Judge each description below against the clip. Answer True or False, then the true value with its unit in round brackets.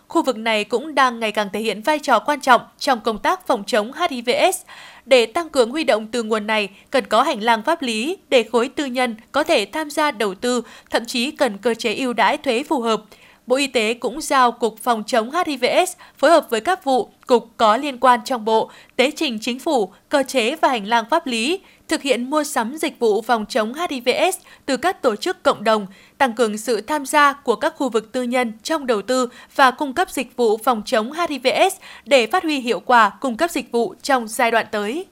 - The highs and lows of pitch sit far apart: False (4.7 semitones)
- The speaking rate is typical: True (230 wpm)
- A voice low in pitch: False (255 Hz)